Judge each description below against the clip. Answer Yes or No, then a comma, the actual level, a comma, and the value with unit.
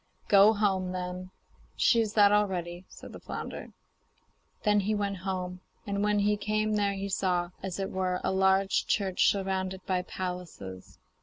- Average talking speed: Yes, average, 160 wpm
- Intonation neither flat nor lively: No, narrow, 1.9 semitones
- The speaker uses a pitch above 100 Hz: Yes, high, 190 Hz